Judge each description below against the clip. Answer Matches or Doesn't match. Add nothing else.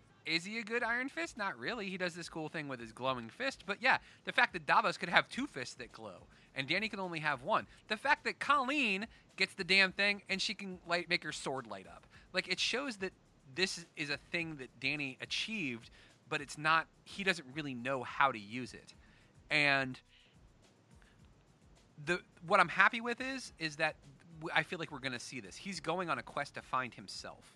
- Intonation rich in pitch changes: Matches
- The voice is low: Doesn't match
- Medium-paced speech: Doesn't match